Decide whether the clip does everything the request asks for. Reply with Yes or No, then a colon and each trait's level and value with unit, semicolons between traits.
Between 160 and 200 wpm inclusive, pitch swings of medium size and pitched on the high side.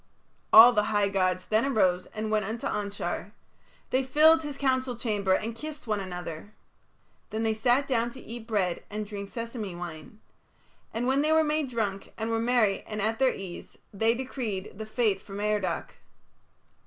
Yes: average, 175 wpm; average, 3.7 semitones; high, 220 Hz